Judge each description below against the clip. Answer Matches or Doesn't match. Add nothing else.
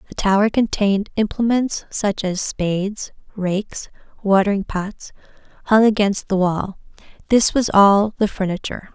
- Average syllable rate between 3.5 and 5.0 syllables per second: Matches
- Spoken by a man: Doesn't match